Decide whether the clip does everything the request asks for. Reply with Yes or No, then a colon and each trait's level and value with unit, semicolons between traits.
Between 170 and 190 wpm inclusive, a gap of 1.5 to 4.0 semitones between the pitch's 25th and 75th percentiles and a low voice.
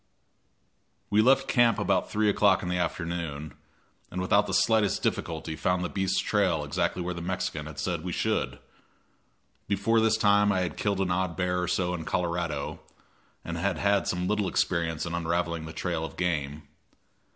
Yes: average, 175 wpm; average, 3.1 semitones; very low, 90 Hz